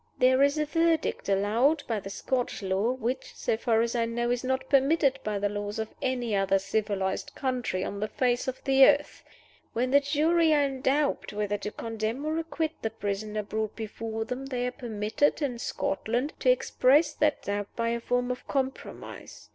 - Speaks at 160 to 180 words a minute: No, average, 190 wpm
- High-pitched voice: Yes, high, 245 Hz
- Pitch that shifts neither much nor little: Yes, average, 4.5 semitones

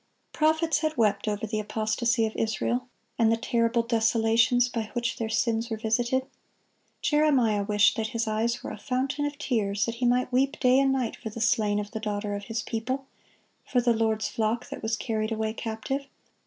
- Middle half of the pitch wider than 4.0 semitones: No, narrow, 2.4 semitones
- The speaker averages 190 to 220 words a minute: Yes, average, 195 wpm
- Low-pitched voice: No, high, 230 Hz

